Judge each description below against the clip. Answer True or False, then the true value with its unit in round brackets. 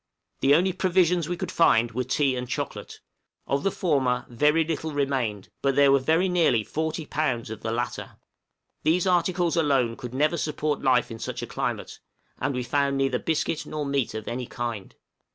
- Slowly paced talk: False (180 wpm)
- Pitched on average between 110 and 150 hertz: True (140 Hz)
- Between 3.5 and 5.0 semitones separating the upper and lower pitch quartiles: True (4.5 semitones)